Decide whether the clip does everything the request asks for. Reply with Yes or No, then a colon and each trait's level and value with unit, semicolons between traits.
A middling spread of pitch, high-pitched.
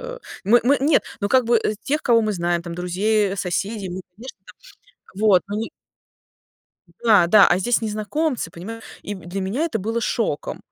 Yes: average, 3.8 semitones; high, 215 Hz